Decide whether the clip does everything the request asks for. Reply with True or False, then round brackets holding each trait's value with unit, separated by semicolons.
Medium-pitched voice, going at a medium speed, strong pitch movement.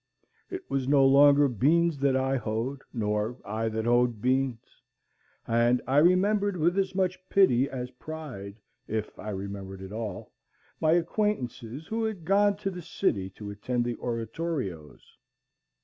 False (130 Hz; 150 wpm; 7.2 semitones)